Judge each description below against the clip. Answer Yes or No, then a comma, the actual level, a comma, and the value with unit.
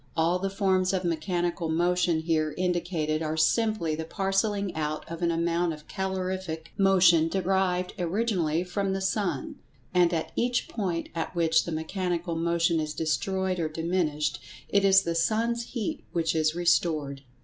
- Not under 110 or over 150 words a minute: No, average, 160 wpm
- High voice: No, medium, 175 Hz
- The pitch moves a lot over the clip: No, average, 2.8 semitones